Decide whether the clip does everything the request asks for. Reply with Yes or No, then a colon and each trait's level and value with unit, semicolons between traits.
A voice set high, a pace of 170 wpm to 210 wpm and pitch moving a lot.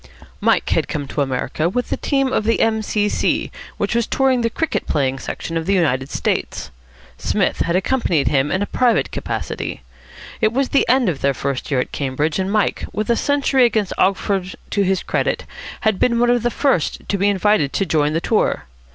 Yes: high, 200 Hz; fast, 205 wpm; wide, 7.6 semitones